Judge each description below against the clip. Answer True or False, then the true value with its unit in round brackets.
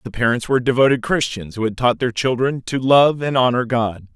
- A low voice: True (125 Hz)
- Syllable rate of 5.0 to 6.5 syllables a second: True (5.6 syllables/s)